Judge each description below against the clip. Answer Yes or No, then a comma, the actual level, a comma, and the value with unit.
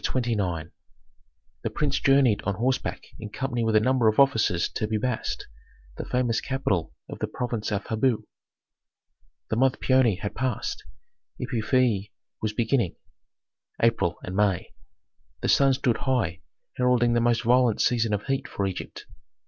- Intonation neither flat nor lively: Yes, average, 3.5 semitones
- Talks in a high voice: No, low, 115 Hz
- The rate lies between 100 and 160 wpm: Yes, average, 150 wpm